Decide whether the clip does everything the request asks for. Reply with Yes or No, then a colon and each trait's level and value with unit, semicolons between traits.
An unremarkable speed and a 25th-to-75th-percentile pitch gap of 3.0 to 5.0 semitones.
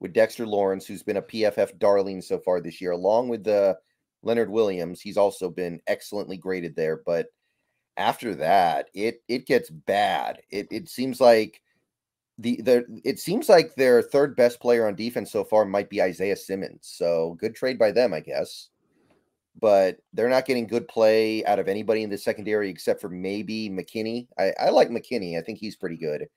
Yes: average, 190 wpm; average, 3.6 semitones